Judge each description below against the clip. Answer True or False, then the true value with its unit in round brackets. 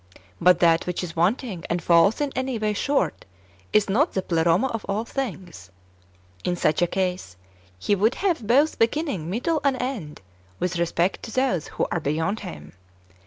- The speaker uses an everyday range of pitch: False (6.6 semitones)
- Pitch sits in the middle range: False (195 Hz)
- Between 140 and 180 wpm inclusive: True (170 wpm)